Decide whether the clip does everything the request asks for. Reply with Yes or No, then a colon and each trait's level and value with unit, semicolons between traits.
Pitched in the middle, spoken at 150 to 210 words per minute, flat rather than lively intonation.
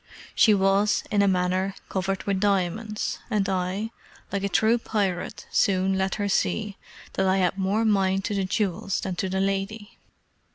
No: high, 195 Hz; average, 170 wpm; narrow, 1.5 semitones